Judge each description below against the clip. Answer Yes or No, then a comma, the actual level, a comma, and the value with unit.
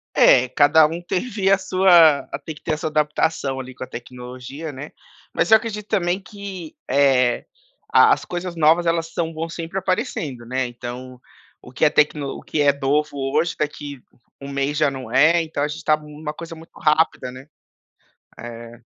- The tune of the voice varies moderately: Yes, average, 3.9 semitones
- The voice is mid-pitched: Yes, medium, 150 Hz